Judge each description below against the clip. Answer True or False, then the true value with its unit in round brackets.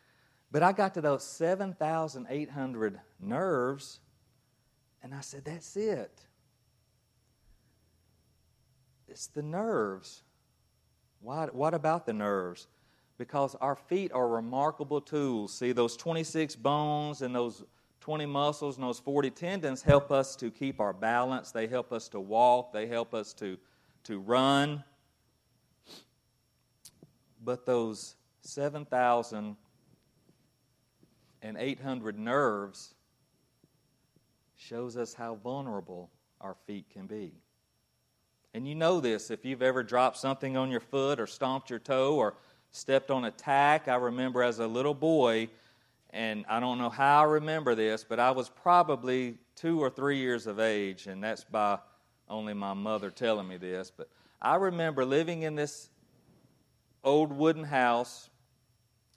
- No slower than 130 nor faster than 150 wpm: True (135 wpm)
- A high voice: False (125 Hz)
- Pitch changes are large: False (3.7 semitones)